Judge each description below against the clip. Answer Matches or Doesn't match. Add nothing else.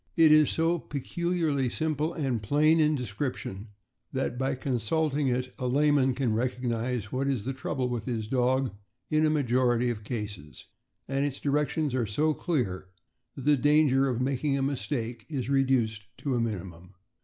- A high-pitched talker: Doesn't match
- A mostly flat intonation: Doesn't match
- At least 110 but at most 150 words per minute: Doesn't match